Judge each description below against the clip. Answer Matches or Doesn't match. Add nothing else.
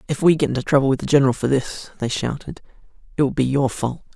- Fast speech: Matches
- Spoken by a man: Matches